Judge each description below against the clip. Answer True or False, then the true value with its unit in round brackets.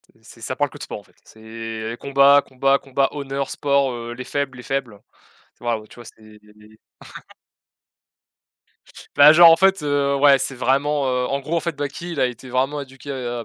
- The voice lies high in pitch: False (135 Hz)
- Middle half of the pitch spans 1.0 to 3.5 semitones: True (2.9 semitones)